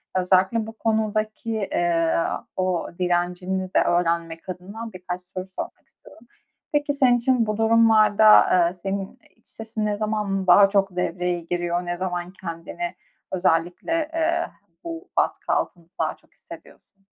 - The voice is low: No, high, 195 Hz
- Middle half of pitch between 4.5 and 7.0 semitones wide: No, average, 3.8 semitones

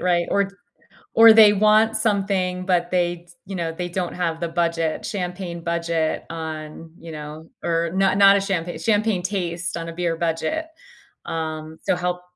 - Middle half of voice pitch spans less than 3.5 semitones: Yes, average, 2.8 semitones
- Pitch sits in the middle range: Yes, medium, 175 Hz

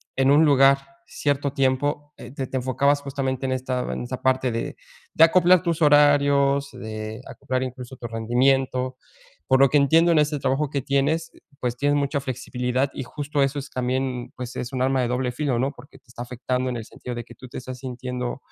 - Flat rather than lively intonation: Yes, narrow, 2.1 semitones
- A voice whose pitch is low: Yes, low, 130 Hz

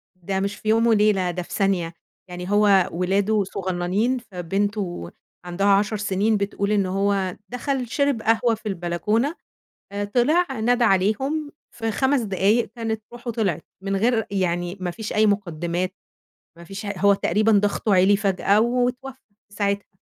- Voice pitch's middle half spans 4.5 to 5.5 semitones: No, average, 3.1 semitones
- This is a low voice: No, high, 205 Hz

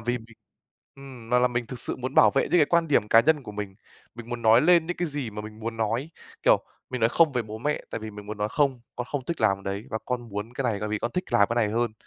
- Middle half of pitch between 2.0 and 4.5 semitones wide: Yes, average, 3.9 semitones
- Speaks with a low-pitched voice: Yes, low, 120 Hz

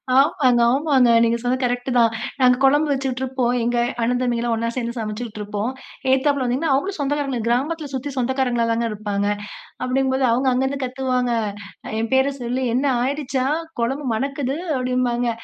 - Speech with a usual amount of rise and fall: No, narrow, 2.1 semitones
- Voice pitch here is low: No, very high, 255 Hz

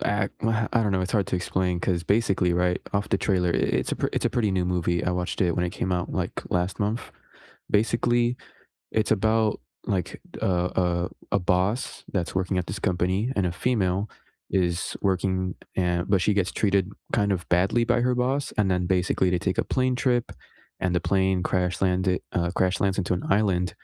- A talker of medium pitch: No, very low, 95 Hz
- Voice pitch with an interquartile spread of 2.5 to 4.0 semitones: Yes, average, 2.8 semitones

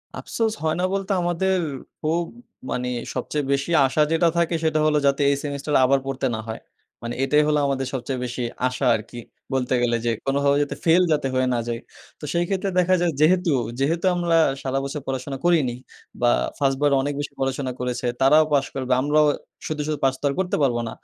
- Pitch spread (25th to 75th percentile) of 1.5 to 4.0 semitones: Yes, average, 3.7 semitones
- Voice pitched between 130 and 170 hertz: Yes, medium, 140 Hz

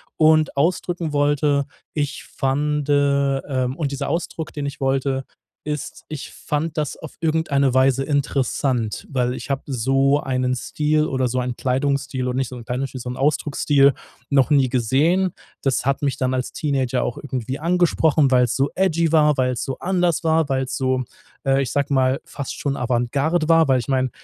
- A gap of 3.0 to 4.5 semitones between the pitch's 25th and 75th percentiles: No, narrow, 2.5 semitones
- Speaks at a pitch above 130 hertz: Yes, medium, 140 Hz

